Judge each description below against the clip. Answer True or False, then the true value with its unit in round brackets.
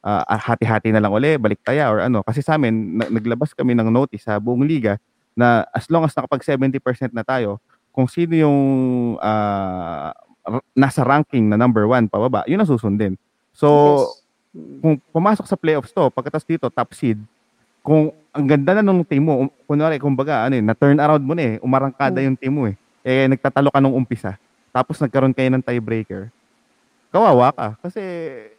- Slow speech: False (175 wpm)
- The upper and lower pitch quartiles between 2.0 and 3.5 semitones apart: False (4.8 semitones)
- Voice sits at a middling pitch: False (130 Hz)